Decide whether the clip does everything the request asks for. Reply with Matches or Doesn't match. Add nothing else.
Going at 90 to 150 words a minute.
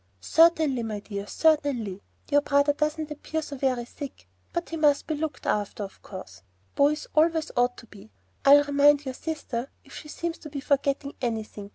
Doesn't match